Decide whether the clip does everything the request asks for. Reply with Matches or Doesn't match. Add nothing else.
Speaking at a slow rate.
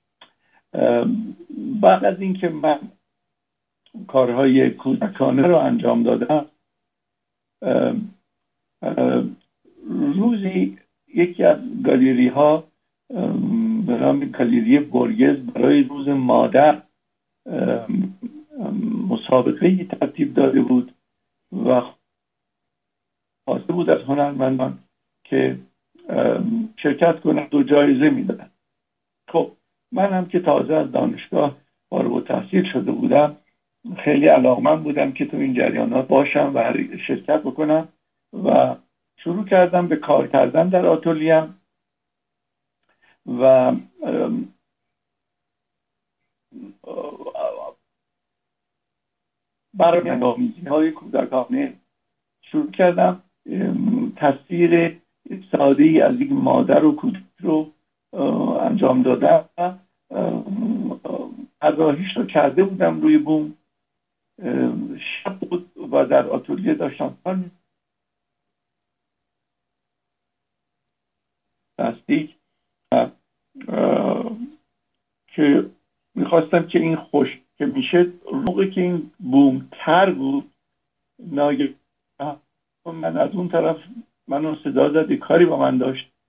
Matches